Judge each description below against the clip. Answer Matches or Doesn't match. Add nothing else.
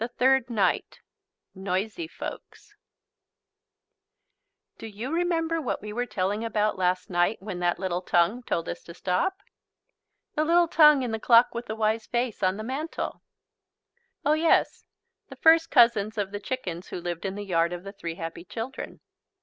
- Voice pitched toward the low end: Doesn't match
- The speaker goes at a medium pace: Matches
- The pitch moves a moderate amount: Doesn't match